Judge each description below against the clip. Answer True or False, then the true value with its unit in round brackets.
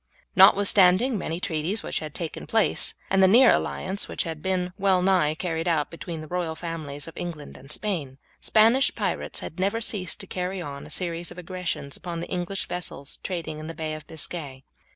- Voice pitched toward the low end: False (175 Hz)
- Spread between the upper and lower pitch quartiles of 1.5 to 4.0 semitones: True (3.2 semitones)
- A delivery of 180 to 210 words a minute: True (195 wpm)